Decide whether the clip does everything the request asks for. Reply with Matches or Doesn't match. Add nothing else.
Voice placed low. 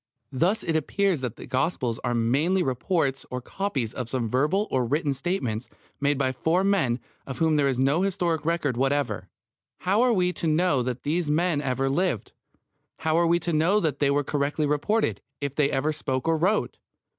Doesn't match